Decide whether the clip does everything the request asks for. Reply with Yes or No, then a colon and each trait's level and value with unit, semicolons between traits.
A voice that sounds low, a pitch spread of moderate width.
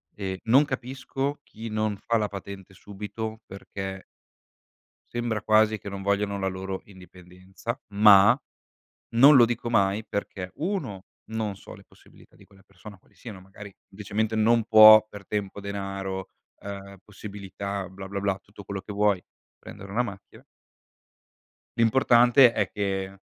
No: low, 100 Hz; narrow, 2.2 semitones